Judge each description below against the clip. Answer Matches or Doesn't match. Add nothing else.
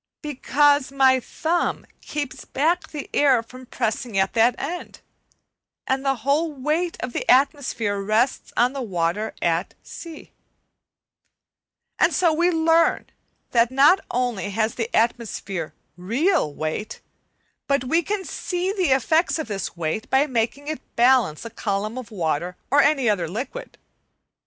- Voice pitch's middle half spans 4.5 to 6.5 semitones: Matches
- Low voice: Doesn't match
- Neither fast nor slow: Matches